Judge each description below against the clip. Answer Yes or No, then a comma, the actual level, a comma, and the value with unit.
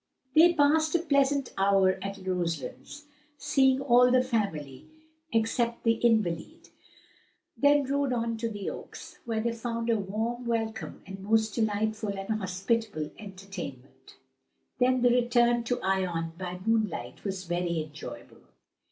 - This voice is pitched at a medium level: No, high, 220 Hz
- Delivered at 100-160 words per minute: Yes, slow, 135 wpm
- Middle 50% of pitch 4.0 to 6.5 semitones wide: Yes, average, 4.3 semitones